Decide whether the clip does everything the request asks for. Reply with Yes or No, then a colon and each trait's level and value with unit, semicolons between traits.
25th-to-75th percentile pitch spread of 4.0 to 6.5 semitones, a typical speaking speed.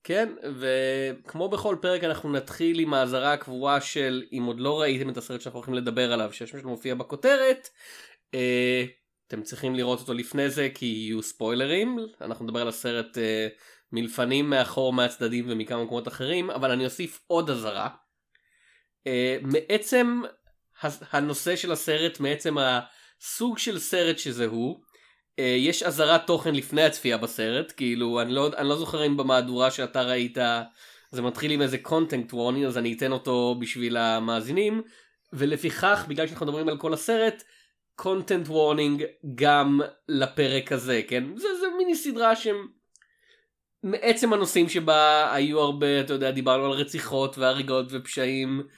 Yes: average, 4.7 semitones; average, 140 wpm